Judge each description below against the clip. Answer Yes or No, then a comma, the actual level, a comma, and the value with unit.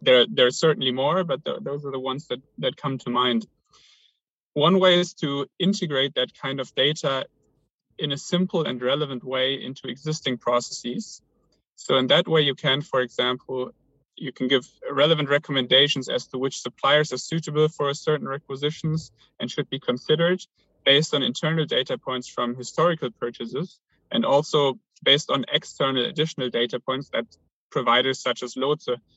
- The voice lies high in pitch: No, low, 135 Hz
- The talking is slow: No, average, 170 wpm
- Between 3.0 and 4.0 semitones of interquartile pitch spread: Yes, average, 3.4 semitones